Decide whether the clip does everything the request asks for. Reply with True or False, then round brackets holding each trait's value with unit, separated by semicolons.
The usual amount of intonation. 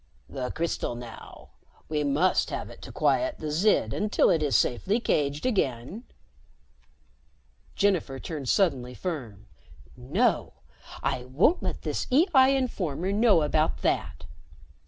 False (7.5 semitones)